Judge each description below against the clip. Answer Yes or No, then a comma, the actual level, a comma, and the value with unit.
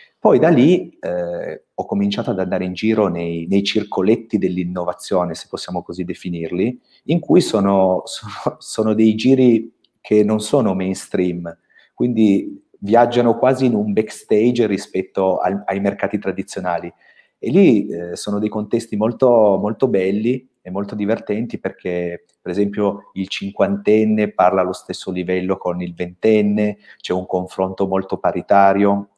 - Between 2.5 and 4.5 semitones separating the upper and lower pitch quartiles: Yes, average, 2.8 semitones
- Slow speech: No, average, 140 wpm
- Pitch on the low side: Yes, low, 100 Hz